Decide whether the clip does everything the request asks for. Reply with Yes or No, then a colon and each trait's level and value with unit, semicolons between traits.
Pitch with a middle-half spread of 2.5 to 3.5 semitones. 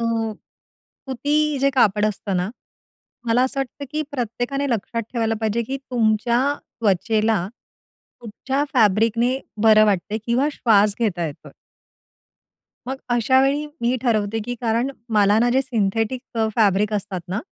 Yes: average, 3.1 semitones